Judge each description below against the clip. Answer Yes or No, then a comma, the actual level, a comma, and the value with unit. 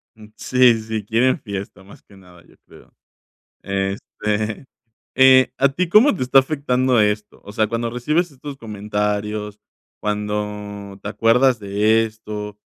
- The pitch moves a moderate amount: Yes, average, 3.6 semitones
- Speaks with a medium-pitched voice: No, low, 110 Hz